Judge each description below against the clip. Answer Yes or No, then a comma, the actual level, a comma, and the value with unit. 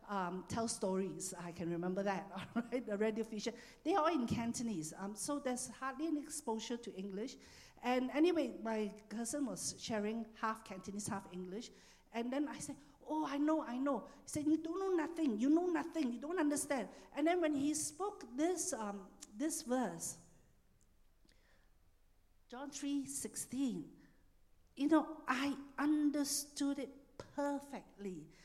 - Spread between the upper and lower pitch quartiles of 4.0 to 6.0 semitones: Yes, average, 5.3 semitones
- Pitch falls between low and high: No, very high, 255 Hz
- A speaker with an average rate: Yes, average, 150 wpm